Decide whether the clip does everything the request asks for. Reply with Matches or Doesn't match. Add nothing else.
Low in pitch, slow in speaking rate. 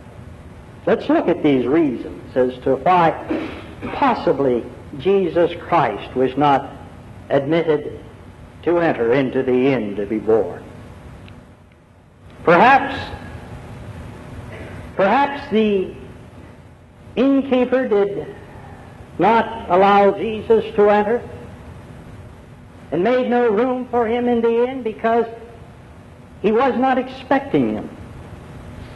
Doesn't match